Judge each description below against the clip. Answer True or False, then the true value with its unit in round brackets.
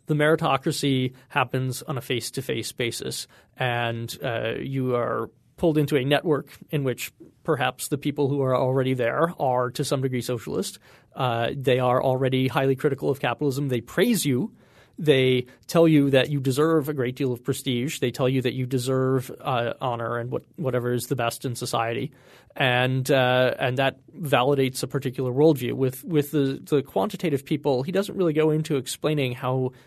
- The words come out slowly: False (175 wpm)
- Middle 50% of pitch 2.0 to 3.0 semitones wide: True (2.5 semitones)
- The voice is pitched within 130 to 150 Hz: True (135 Hz)